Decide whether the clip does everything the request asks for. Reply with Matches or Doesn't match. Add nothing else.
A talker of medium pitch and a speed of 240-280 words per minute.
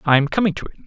Matches